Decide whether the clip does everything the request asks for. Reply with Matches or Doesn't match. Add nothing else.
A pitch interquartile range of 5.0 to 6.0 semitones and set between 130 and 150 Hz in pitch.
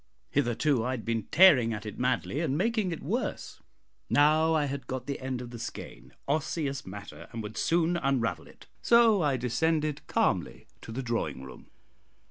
Matches